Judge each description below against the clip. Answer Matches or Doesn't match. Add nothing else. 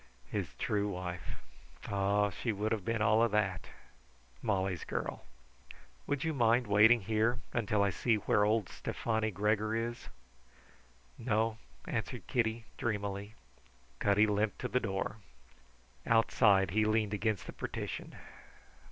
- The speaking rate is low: Matches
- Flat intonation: Matches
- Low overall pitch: Matches